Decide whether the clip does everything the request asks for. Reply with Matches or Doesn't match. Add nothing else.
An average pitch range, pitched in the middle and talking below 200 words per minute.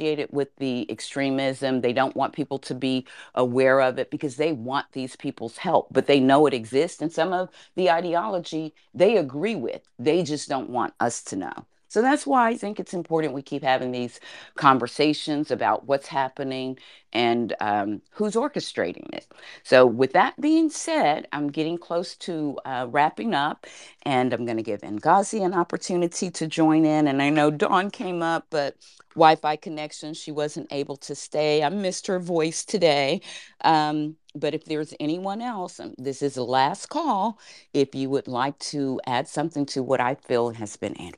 Matches